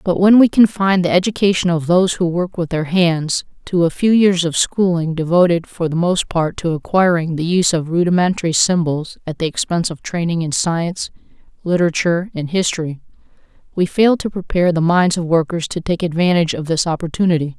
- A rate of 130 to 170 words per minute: No, average, 190 wpm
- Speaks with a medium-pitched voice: Yes, medium, 170 Hz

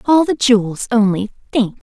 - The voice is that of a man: No, female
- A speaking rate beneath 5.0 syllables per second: Yes, 4.8 syllables/s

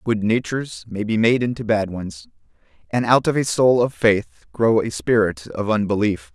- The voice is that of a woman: No, male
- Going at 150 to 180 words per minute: No, average, 190 wpm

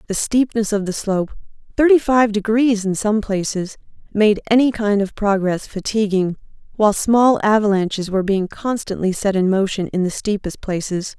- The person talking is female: Yes, female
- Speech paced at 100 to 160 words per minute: Yes, average, 150 wpm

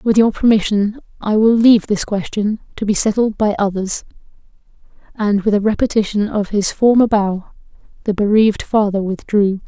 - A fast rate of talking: No, average, 155 wpm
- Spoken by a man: No, female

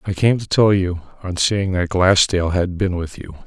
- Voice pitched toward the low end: Yes, very low, 95 Hz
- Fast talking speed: Yes, fast, 210 wpm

